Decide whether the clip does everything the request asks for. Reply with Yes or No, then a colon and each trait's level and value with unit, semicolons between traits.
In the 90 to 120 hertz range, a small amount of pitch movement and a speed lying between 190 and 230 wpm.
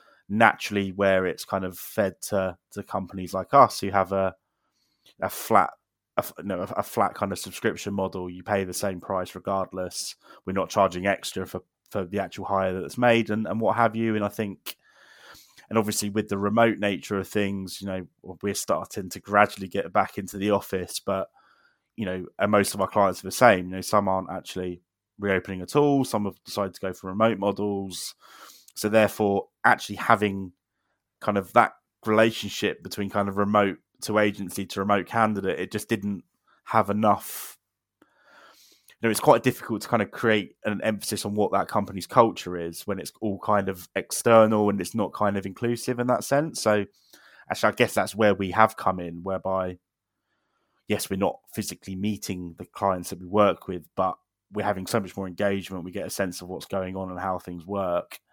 Yes: low, 100 Hz; narrow, 2.0 semitones; average, 195 wpm